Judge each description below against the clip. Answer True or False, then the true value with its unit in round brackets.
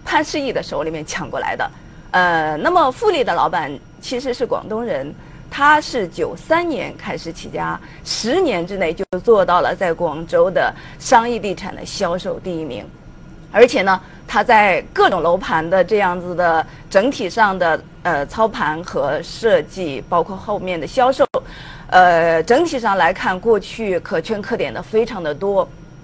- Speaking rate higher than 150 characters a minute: True (240 characters per minute)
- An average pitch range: False (6.1 semitones)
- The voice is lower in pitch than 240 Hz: True (190 Hz)